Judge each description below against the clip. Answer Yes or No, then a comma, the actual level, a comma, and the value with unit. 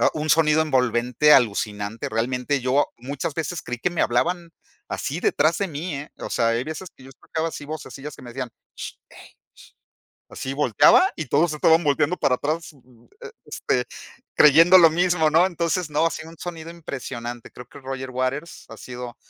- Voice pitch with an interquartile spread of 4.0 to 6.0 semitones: Yes, average, 4.5 semitones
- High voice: No, medium, 150 Hz